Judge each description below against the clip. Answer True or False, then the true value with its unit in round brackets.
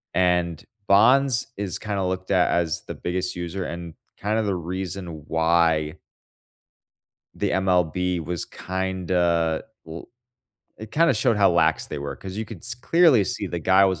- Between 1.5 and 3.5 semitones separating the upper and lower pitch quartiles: True (2.7 semitones)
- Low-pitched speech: True (90 Hz)